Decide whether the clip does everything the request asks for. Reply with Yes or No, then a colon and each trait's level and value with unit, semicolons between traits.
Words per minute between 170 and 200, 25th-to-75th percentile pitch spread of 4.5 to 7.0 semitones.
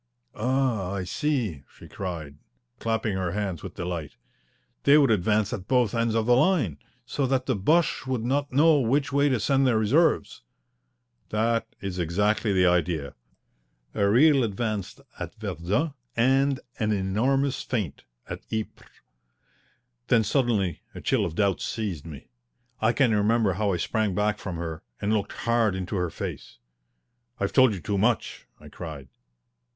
No: average, 155 wpm; wide, 5.4 semitones